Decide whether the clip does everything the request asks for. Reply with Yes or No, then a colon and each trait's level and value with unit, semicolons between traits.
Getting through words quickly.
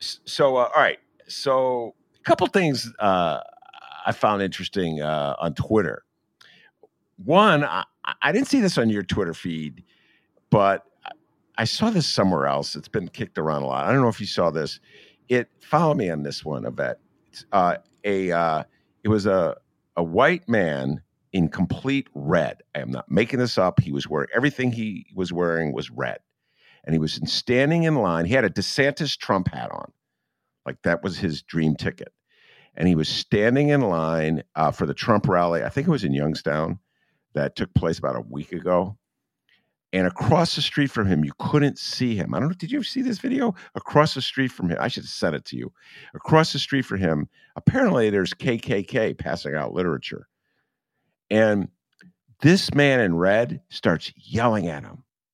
No: average, 185 wpm